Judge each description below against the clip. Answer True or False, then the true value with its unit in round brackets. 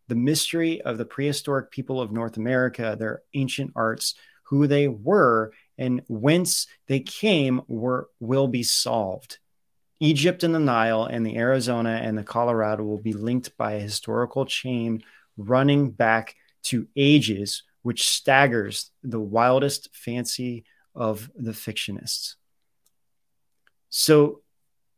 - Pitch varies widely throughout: False (3.9 semitones)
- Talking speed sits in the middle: False (125 wpm)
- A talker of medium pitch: False (125 Hz)